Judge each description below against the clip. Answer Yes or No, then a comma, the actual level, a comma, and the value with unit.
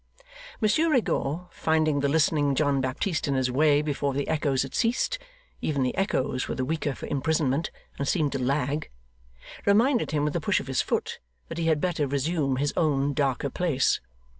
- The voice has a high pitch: No, medium, 145 Hz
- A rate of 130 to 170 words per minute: No, average, 185 wpm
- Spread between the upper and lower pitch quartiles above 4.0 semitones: No, average, 2.9 semitones